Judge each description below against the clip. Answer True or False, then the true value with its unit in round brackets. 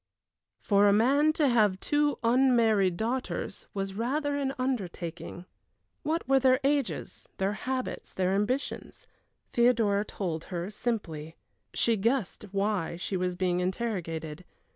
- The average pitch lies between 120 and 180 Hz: False (215 Hz)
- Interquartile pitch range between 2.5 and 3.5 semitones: False (5.6 semitones)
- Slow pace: True (125 wpm)